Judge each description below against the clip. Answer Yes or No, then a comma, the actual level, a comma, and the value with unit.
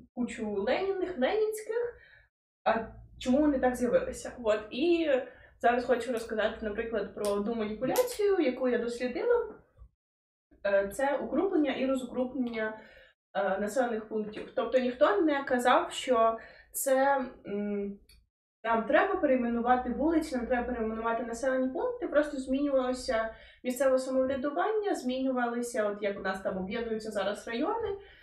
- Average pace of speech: Yes, average, 115 wpm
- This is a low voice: No, very high, 255 Hz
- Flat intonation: No, average, 4.1 semitones